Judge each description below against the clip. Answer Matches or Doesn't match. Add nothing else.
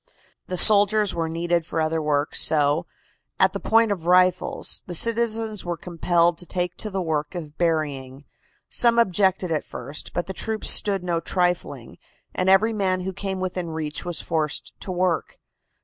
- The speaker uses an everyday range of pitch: Matches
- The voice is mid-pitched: Matches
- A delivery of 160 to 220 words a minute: Matches